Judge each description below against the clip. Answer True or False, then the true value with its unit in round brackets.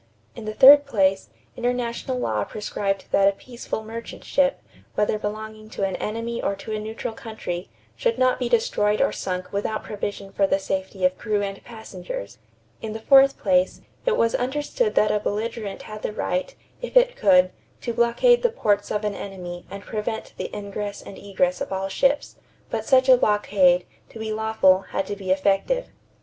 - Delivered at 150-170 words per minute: False (185 wpm)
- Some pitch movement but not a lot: True (3.3 semitones)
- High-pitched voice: True (215 Hz)